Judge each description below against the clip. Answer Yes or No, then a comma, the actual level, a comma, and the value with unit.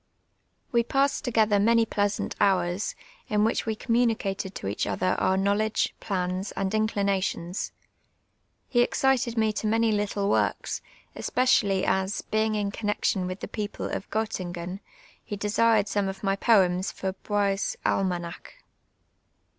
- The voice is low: No, high, 205 Hz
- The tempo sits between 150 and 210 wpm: No, slow, 135 wpm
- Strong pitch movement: No, narrow, 2.4 semitones